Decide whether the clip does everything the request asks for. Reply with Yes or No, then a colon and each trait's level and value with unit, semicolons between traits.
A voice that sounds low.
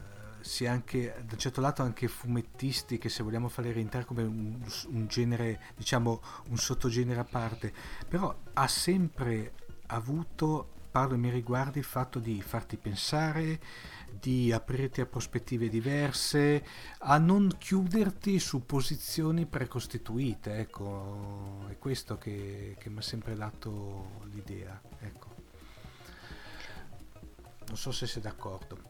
Yes: low, 120 Hz